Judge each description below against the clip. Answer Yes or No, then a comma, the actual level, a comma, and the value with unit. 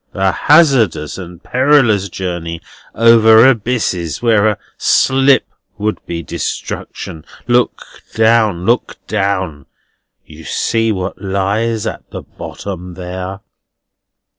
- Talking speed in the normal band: No, slow, 105 wpm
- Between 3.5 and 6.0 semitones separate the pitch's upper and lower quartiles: Yes, average, 4.1 semitones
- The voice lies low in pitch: Yes, low, 105 Hz